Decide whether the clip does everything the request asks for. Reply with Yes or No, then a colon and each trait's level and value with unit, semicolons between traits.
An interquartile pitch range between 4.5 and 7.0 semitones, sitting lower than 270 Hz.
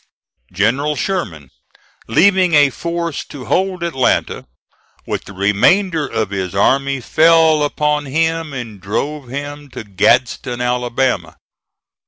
Yes: average, 5.3 semitones; medium, 140 Hz